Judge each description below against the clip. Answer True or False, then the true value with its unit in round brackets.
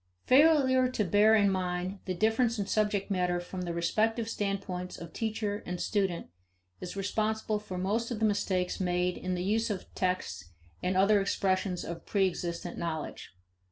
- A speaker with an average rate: True (160 wpm)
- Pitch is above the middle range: True (195 Hz)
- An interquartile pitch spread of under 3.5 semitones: True (3.1 semitones)